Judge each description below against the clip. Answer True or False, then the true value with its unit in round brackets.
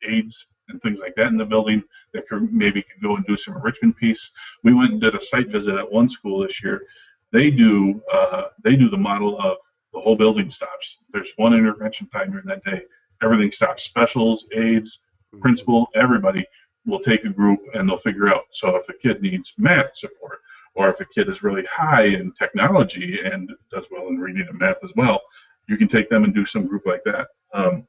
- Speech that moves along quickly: True (215 wpm)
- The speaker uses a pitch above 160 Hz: True (185 Hz)